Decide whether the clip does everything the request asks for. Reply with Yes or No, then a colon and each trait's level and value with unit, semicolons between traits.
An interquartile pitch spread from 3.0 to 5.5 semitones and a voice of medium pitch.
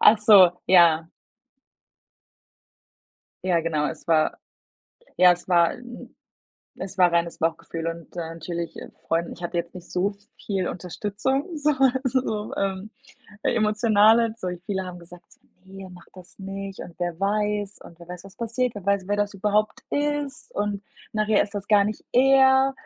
No: average, 3.5 semitones; high, 195 Hz